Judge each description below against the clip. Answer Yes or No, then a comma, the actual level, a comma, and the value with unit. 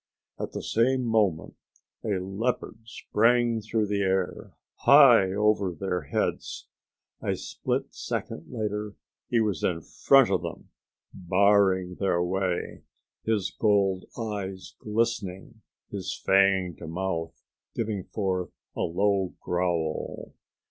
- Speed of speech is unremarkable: No, slow, 115 wpm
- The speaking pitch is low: Yes, low, 100 Hz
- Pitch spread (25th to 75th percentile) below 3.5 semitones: Yes, average, 2.9 semitones